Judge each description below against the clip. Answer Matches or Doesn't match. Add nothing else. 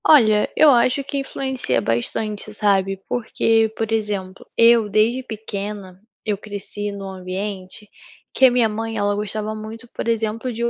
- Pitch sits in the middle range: Doesn't match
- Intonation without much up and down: Matches